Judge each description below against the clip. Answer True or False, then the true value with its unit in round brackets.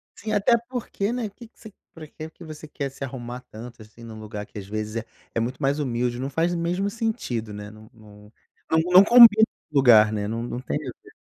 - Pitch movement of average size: False (8.1 semitones)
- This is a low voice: True (130 Hz)